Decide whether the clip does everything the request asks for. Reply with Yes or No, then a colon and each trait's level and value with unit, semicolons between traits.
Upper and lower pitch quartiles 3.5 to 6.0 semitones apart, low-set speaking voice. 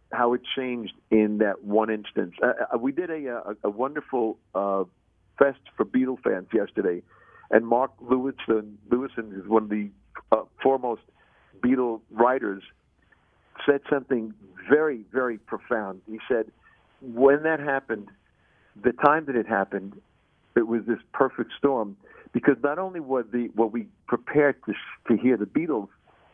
Yes: average, 4.1 semitones; low, 120 Hz